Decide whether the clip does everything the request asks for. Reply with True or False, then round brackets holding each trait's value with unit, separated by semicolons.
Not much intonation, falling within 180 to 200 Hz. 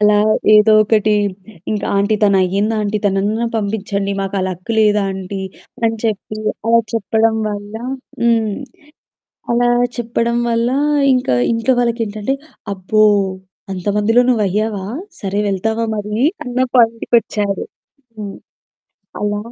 False (2.1 semitones; 210 Hz)